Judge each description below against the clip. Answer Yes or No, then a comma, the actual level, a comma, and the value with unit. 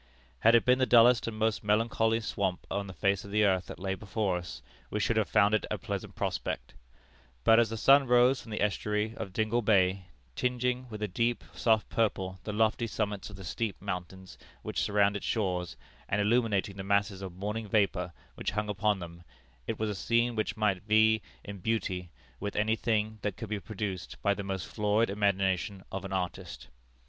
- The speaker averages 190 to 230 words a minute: Yes, average, 200 wpm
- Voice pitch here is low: Yes, low, 105 Hz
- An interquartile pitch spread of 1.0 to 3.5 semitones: Yes, narrow, 2.6 semitones